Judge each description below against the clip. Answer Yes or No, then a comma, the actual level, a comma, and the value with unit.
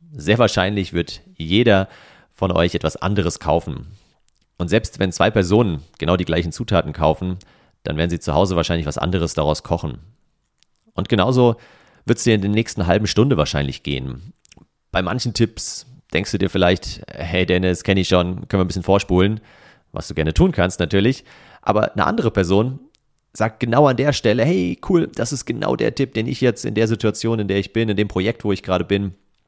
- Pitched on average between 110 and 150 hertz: No, low, 100 Hz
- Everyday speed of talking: No, fast, 195 wpm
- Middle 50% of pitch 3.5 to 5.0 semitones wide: Yes, average, 4.4 semitones